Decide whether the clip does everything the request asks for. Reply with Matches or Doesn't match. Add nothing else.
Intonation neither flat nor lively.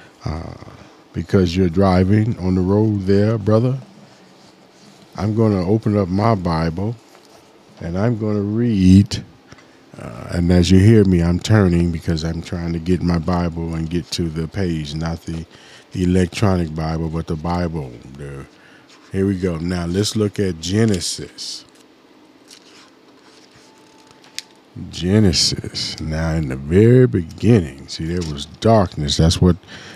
Matches